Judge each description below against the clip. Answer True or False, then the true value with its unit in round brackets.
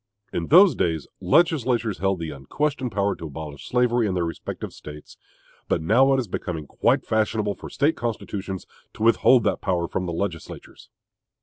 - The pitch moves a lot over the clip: True (6.4 semitones)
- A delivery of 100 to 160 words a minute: False (170 wpm)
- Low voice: True (100 Hz)